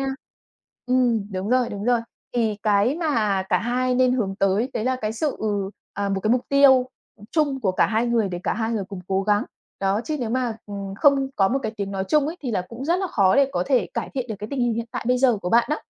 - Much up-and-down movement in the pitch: No, average, 4.1 semitones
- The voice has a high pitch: Yes, high, 230 Hz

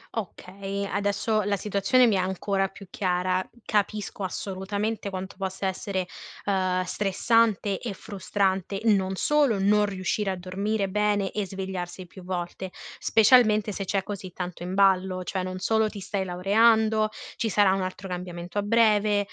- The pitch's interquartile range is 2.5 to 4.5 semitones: No, narrow, 1.9 semitones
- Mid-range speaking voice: No, high, 195 Hz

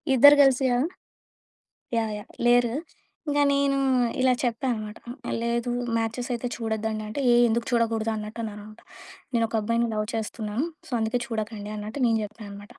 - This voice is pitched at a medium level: No, high, 230 Hz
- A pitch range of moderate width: No, narrow, 2.1 semitones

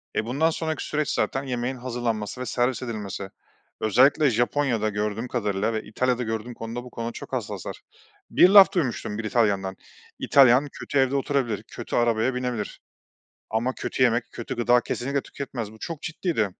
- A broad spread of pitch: No, average, 3.2 semitones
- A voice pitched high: No, low, 120 Hz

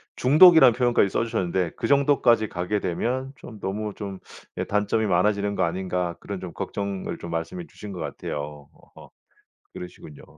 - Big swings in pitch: No, average, 4.7 semitones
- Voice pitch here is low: Yes, low, 100 Hz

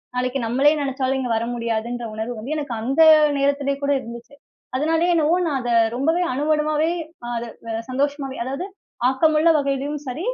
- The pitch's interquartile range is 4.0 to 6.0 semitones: No, average, 3.3 semitones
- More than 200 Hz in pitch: Yes, very high, 275 Hz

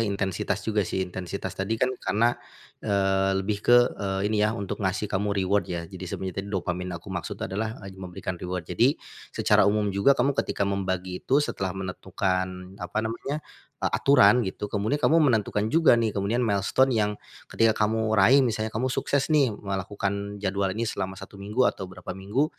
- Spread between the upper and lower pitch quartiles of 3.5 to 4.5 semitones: No, average, 2.8 semitones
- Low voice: Yes, low, 100 Hz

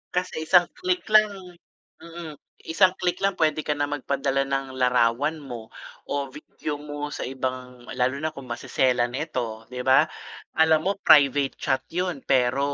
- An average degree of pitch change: Yes, average, 3.9 semitones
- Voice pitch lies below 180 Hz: Yes, medium, 140 Hz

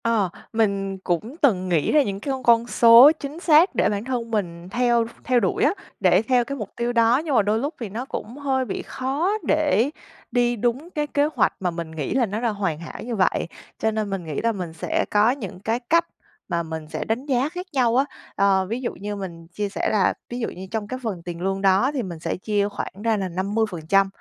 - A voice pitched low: No, high, 220 Hz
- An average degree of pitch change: Yes, average, 4.8 semitones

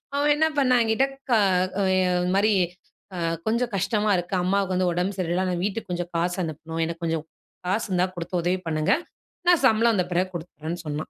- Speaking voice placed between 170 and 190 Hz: Yes, medium, 185 Hz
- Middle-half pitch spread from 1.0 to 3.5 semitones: No, average, 4.0 semitones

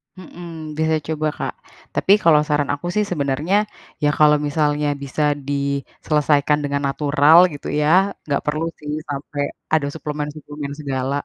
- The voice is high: No, medium, 150 Hz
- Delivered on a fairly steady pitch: Yes, narrow, 1.5 semitones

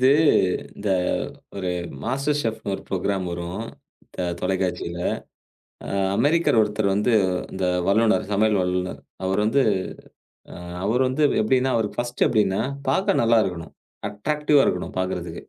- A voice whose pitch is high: No, low, 105 Hz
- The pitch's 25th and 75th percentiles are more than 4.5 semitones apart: Yes, average, 5.2 semitones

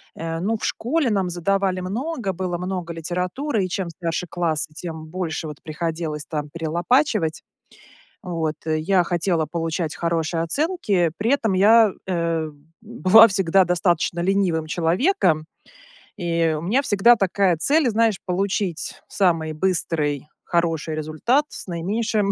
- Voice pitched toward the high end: No, medium, 175 Hz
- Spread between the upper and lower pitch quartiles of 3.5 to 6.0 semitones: Yes, average, 3.8 semitones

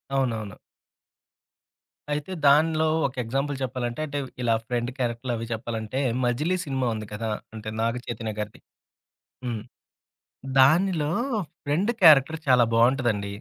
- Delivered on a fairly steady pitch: No, average, 4.1 semitones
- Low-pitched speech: Yes, low, 125 Hz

